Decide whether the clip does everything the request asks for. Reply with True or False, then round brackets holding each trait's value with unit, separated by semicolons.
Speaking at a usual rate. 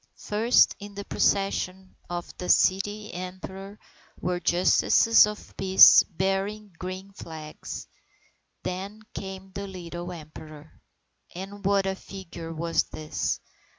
False (120 wpm)